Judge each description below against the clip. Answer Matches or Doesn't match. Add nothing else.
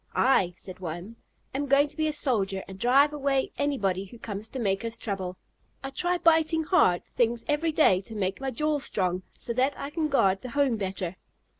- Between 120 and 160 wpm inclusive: Doesn't match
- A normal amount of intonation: Doesn't match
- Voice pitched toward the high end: Matches